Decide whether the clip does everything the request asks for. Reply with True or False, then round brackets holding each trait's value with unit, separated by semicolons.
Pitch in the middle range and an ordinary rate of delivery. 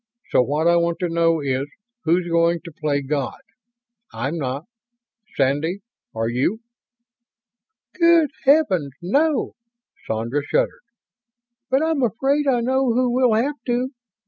False (170 Hz; 130 wpm)